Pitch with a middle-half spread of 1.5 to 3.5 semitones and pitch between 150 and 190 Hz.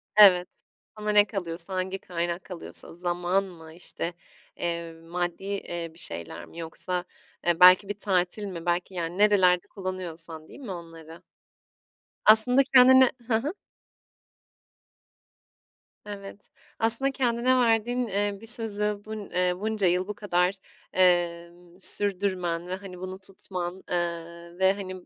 Yes: average, 3.0 semitones; medium, 185 Hz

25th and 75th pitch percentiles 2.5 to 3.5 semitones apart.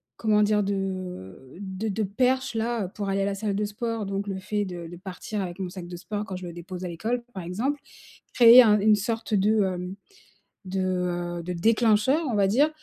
Yes: average, 3.1 semitones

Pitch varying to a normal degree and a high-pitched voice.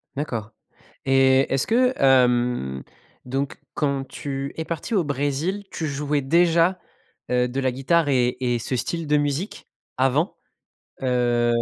No: average, 3.7 semitones; low, 135 Hz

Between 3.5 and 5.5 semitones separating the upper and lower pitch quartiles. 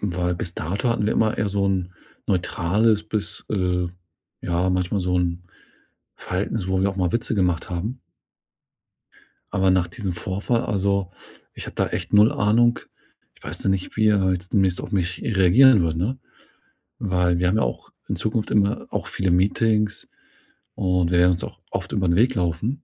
No: average, 2.9 semitones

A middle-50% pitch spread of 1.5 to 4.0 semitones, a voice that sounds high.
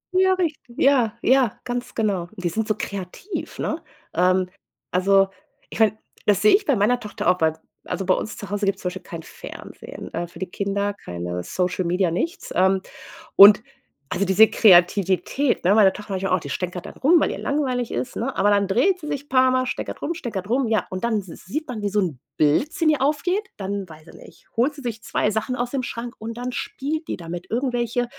No: wide, 5.4 semitones; high, 210 Hz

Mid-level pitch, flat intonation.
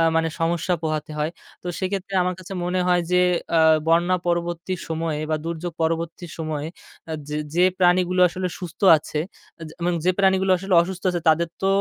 Yes: medium, 175 Hz; narrow, 2.0 semitones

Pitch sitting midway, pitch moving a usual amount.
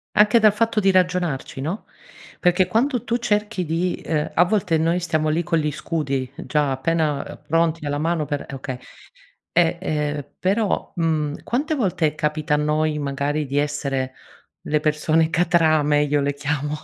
Yes: medium, 155 Hz; average, 3.3 semitones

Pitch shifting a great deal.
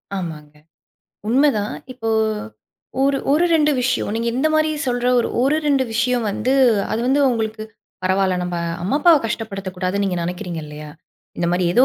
Yes: wide, 6.3 semitones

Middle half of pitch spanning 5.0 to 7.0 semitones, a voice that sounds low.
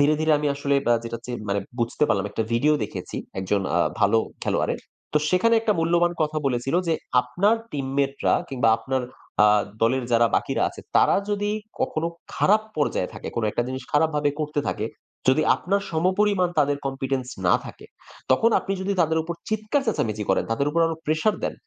No: wide, 5.6 semitones; medium, 145 Hz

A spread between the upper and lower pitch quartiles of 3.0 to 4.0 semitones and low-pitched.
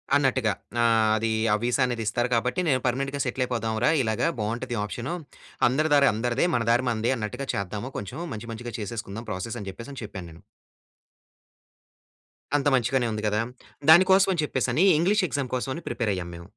Yes: average, 3.7 semitones; low, 120 Hz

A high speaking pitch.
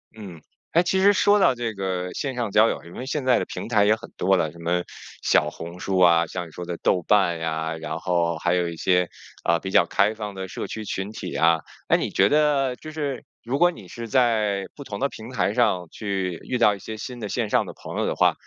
No: low, 100 Hz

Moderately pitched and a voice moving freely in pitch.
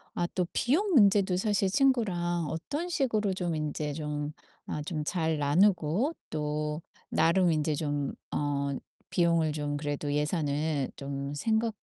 No: medium, 160 Hz; average, 4.8 semitones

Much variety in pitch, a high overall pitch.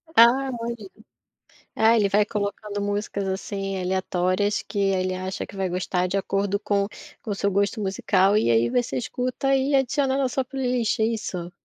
No: average, 3.5 semitones; high, 200 Hz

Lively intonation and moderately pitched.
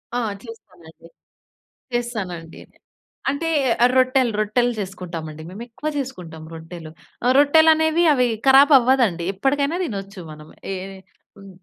No: wide, 7.2 semitones; high, 230 Hz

